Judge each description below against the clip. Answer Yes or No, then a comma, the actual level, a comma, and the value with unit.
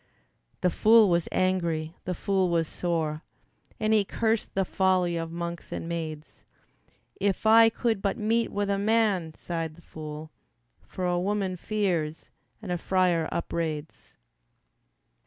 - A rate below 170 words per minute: Yes, average, 140 wpm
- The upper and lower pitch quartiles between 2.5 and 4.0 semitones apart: Yes, average, 3.5 semitones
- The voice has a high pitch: No, medium, 180 Hz